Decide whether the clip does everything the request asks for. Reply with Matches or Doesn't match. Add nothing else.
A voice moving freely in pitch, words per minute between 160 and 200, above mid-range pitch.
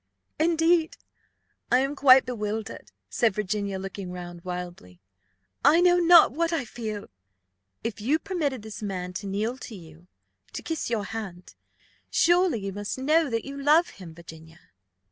Doesn't match